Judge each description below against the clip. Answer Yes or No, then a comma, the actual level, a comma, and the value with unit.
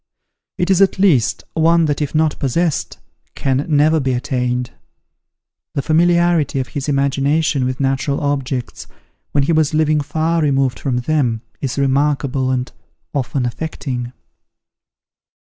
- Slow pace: Yes, slow, 130 wpm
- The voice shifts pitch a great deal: No, average, 3.2 semitones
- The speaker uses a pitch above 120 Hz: Yes, medium, 140 Hz